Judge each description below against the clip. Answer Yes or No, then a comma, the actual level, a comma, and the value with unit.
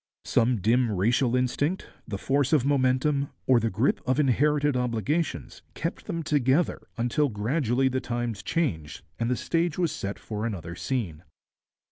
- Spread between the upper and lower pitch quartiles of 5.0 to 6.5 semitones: No, average, 4.2 semitones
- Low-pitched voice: Yes, low, 125 Hz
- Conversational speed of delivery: Yes, average, 150 wpm